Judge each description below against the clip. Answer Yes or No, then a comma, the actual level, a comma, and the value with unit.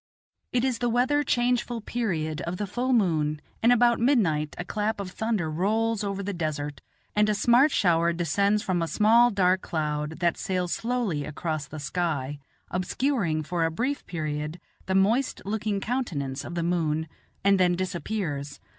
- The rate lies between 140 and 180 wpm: Yes, average, 165 wpm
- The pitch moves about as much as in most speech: No, wide, 6.2 semitones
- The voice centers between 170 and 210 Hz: Yes, medium, 185 Hz